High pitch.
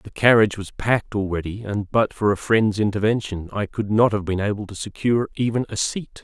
No: low, 105 Hz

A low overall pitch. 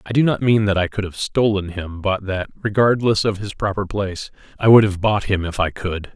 Yes: low, 100 Hz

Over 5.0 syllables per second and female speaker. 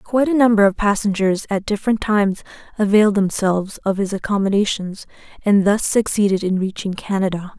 Yes: 5.8 syllables/s; female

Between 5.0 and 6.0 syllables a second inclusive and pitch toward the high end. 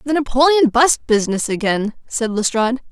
Yes: 5.6 syllables/s; high, 245 Hz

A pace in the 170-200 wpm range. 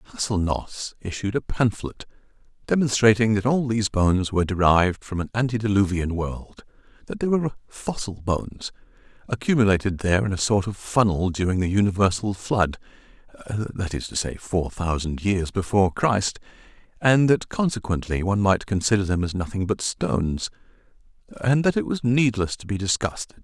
No: average, 150 wpm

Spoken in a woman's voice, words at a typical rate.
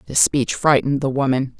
Yes: female; average, 190 wpm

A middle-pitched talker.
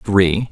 No: very low, 95 Hz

